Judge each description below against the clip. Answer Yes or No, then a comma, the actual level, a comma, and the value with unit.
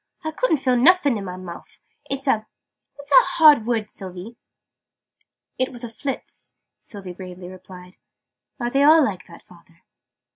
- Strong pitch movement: Yes, wide, 7.0 semitones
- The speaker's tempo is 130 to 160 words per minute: Yes, average, 155 wpm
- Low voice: No, high, 225 Hz